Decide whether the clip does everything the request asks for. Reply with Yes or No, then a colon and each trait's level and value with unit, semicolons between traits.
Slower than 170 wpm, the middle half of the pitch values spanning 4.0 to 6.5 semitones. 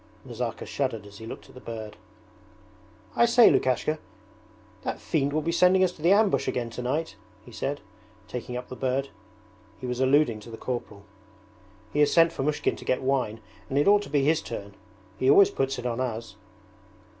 No: average, 190 wpm; average, 4.4 semitones